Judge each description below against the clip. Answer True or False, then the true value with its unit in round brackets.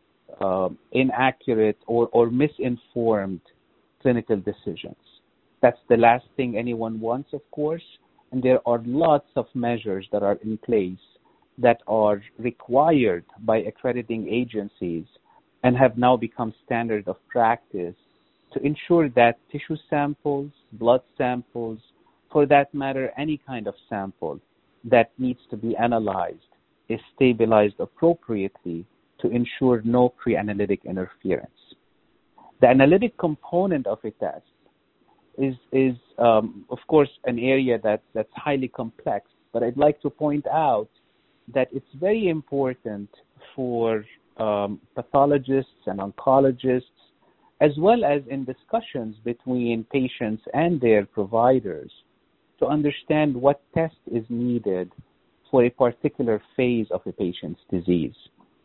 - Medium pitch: False (125 Hz)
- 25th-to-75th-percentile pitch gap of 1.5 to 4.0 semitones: True (3.7 semitones)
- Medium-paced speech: False (125 wpm)